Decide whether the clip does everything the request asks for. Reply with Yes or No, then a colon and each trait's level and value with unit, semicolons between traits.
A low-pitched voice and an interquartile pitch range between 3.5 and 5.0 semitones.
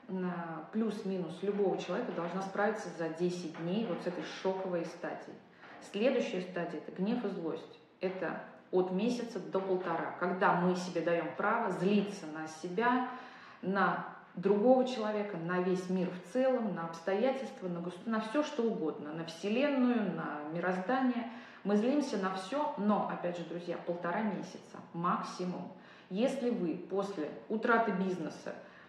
No: high, 190 Hz; average, 4.1 semitones